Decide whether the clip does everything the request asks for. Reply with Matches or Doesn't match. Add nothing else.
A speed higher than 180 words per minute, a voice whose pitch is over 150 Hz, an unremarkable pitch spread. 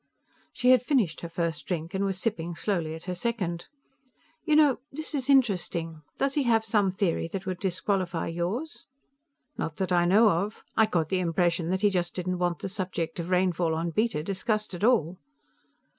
Matches